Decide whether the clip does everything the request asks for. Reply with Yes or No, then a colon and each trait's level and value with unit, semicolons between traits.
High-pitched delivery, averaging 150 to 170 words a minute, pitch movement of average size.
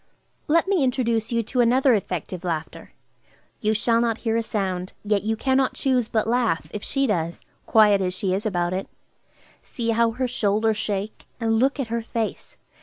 No: high, 225 Hz; average, 185 wpm; average, 3.2 semitones